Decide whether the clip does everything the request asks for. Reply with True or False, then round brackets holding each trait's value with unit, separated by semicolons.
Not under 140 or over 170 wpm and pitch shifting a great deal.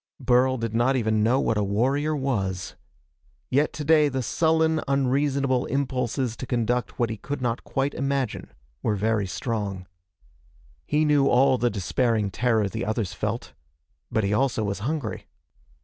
False (150 wpm; 4.0 semitones)